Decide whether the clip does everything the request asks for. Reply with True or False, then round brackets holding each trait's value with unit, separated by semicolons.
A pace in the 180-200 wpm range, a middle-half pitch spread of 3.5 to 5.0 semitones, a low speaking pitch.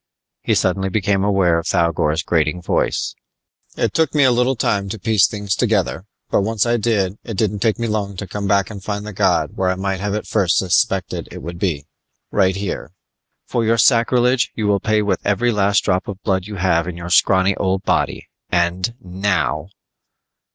False (195 wpm; 2.7 semitones; 100 Hz)